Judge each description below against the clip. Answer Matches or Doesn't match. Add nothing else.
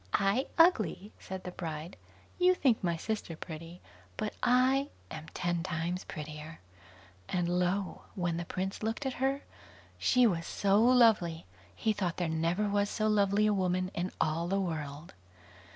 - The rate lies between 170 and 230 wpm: Doesn't match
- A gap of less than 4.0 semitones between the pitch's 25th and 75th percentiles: Doesn't match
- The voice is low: Doesn't match